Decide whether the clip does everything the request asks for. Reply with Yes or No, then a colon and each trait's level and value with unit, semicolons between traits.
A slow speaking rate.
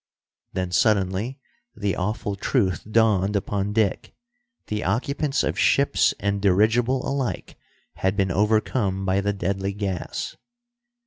Yes: slow, 120 wpm